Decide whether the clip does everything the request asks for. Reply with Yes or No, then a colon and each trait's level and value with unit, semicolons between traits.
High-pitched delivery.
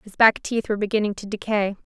Yes: high, 210 Hz